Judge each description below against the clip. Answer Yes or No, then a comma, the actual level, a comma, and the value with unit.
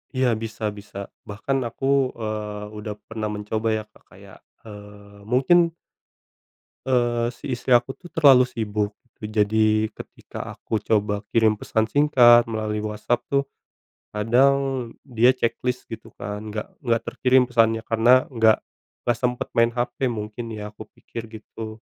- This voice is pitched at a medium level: No, low, 115 Hz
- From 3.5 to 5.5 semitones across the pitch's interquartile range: No, average, 2.7 semitones